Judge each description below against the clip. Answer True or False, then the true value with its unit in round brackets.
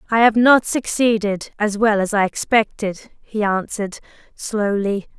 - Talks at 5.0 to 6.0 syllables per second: False (4.5 syllables/s)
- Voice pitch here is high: True (215 Hz)